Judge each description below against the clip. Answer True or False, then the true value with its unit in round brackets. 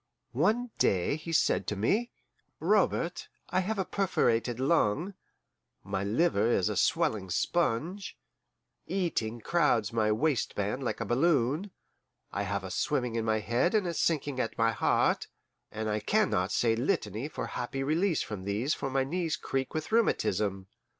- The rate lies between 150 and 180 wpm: True (155 wpm)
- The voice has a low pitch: True (130 Hz)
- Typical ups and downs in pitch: False (7.7 semitones)